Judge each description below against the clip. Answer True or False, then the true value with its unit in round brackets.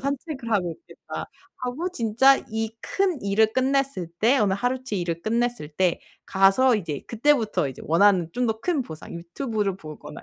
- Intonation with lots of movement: True (5.8 semitones)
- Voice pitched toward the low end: False (220 Hz)